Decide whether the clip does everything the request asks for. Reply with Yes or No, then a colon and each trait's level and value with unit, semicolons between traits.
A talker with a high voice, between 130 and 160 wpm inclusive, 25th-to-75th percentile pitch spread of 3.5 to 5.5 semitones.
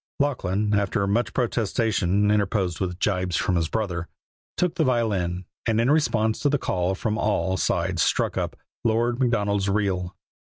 No: low, 105 Hz; average, 155 wpm; average, 3.8 semitones